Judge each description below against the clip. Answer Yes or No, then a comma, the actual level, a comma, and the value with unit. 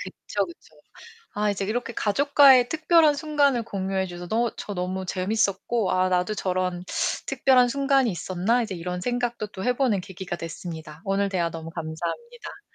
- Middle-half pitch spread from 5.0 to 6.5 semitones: Yes, wide, 5.4 semitones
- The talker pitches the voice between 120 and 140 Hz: No, high, 200 Hz